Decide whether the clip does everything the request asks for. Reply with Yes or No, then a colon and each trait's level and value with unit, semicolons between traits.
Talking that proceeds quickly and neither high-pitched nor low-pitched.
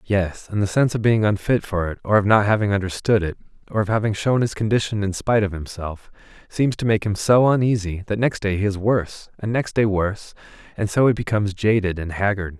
No: fast, 230 wpm; low, 105 Hz